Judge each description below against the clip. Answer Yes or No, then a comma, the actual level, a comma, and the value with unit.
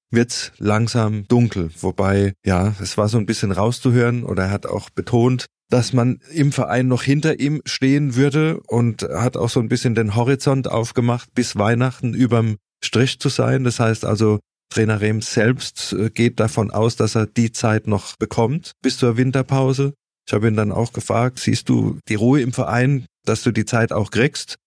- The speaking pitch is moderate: No, low, 120 Hz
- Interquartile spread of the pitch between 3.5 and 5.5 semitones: No, average, 2.9 semitones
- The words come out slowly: No, average, 185 wpm